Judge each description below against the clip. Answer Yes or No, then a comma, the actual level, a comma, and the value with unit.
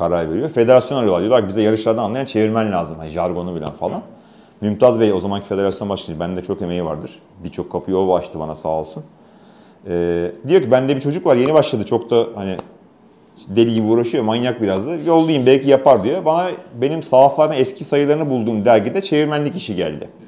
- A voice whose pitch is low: Yes, low, 110 Hz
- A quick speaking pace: Yes, fast, 185 wpm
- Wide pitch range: Yes, wide, 7.2 semitones